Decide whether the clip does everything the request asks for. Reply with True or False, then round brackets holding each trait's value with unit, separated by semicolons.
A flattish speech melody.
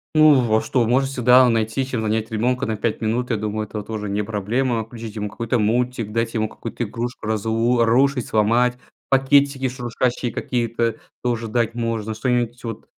True (2.2 semitones)